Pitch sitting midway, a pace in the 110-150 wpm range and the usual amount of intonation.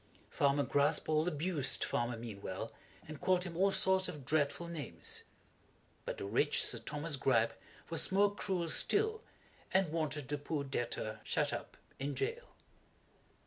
Yes: medium, 150 Hz; average, 145 wpm; average, 4.7 semitones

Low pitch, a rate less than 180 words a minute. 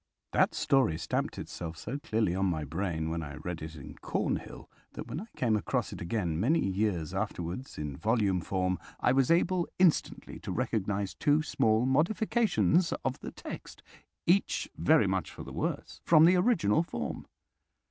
Yes: low, 105 Hz; average, 160 wpm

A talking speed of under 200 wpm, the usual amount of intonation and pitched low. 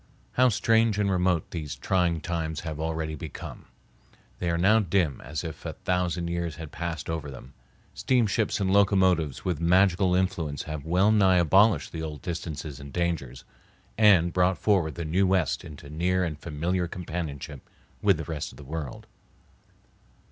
Yes: average, 160 wpm; average, 3.2 semitones; very low, 85 Hz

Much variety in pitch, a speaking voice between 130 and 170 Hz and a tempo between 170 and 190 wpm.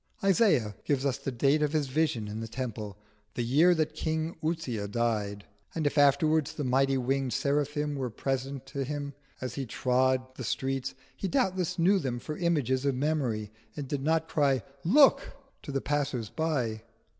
No: average, 3.5 semitones; low, 135 Hz; average, 175 wpm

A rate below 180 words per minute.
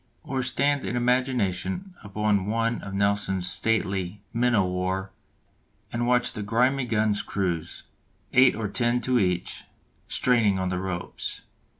Yes: slow, 135 wpm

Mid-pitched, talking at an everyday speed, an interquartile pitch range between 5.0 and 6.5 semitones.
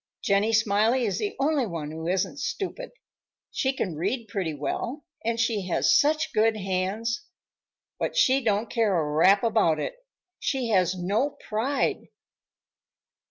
No: high, 220 Hz; average, 145 wpm; wide, 5.5 semitones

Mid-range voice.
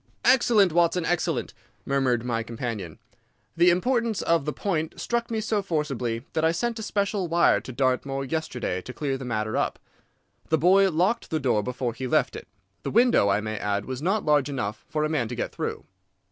Yes: medium, 150 Hz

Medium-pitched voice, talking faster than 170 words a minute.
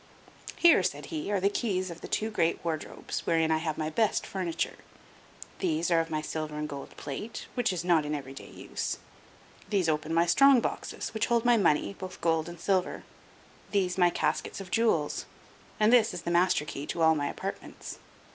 Yes: medium, 170 Hz; average, 195 wpm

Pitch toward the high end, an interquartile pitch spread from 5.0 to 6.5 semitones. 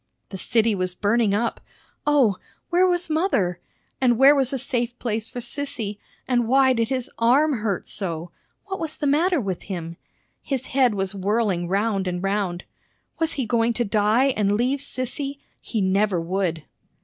Yes: high, 230 Hz; wide, 5.4 semitones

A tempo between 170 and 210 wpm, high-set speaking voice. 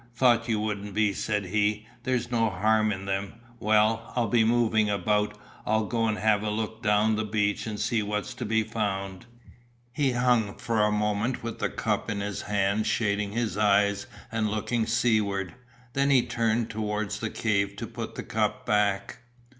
No: average, 180 wpm; low, 105 Hz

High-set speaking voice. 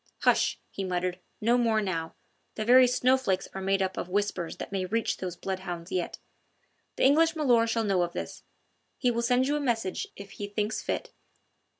Yes: high, 205 Hz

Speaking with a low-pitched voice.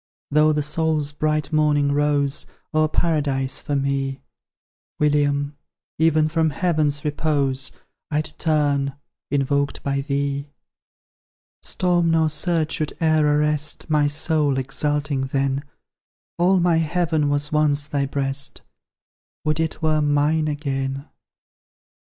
No: medium, 150 Hz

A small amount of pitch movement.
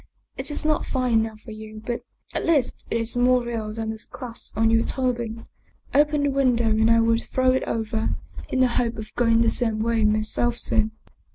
Yes: narrow, 2.2 semitones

